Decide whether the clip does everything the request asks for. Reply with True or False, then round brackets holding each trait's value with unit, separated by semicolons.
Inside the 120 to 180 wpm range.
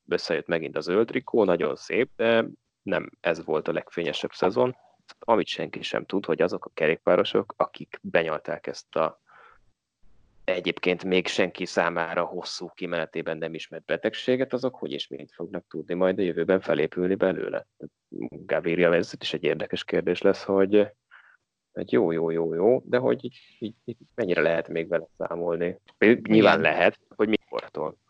True (150 wpm)